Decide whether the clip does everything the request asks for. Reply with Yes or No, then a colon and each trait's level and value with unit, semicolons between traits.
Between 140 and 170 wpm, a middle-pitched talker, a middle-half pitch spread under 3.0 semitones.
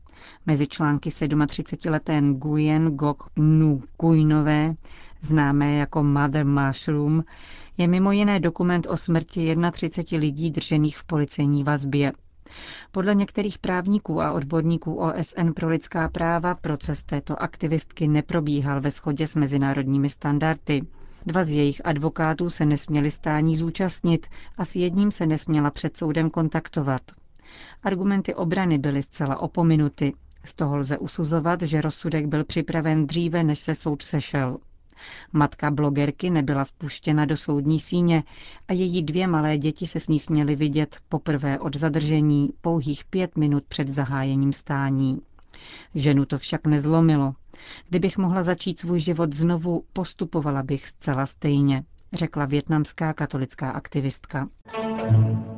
No: average, 125 wpm; medium, 155 Hz; narrow, 2.5 semitones